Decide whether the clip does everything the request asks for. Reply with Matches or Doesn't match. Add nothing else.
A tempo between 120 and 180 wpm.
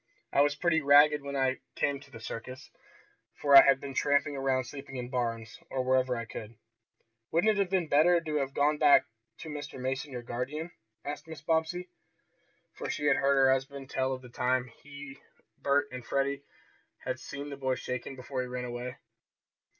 Doesn't match